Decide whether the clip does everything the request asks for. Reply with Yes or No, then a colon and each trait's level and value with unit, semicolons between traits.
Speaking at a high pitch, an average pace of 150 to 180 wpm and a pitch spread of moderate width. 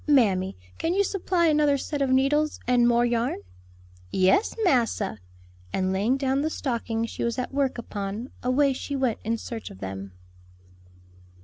Yes: very high, 250 Hz; average, 155 wpm; average, 4.2 semitones